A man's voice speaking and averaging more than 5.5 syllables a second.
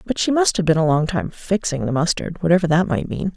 No: female; 5.9 syllables/s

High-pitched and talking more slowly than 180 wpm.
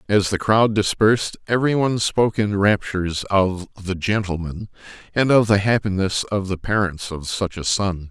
No: low, 100 Hz; average, 170 wpm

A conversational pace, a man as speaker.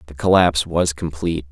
Yes: average, 160 wpm; male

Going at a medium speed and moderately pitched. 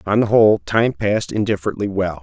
No: average, 190 wpm; low, 100 Hz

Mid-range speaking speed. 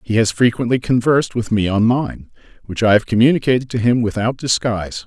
Yes: average, 190 wpm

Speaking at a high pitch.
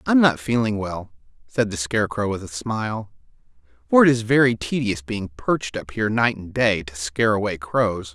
No: low, 105 Hz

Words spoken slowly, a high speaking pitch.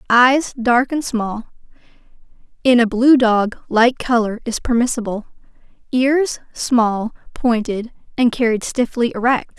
Yes: slow, 105 wpm; high, 240 Hz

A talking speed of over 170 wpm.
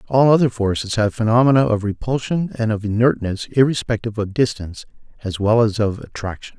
No: average, 165 wpm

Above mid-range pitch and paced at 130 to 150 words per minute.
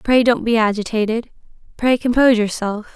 Yes: high, 230 Hz; average, 140 wpm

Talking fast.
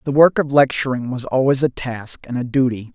Yes: fast, 225 wpm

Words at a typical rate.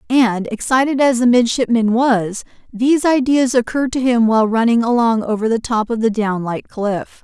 Yes: average, 180 wpm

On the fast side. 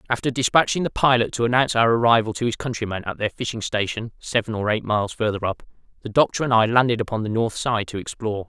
Yes: fast, 225 wpm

